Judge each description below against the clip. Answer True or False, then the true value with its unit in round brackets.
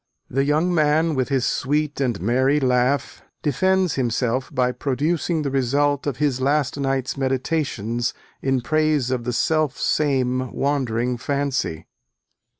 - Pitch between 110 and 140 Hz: True (135 Hz)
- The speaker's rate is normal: False (130 wpm)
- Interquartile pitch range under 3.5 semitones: True (2.8 semitones)